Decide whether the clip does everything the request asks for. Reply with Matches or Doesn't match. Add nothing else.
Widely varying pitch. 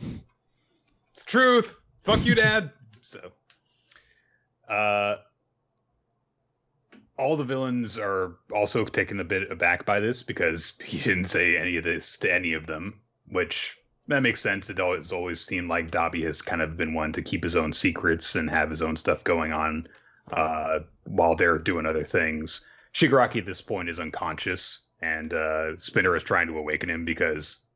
Matches